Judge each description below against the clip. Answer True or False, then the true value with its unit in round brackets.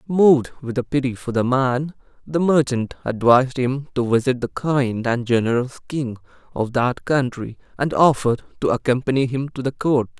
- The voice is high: False (130 Hz)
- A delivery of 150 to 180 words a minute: True (165 wpm)